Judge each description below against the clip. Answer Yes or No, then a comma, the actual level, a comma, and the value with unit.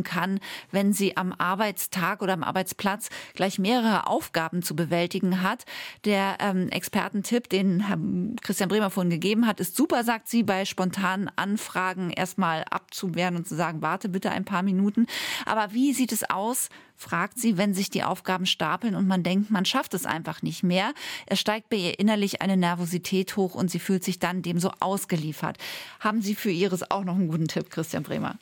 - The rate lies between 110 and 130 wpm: No, fast, 190 wpm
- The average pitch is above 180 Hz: Yes, high, 190 Hz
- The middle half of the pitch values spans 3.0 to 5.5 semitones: No, narrow, 2.4 semitones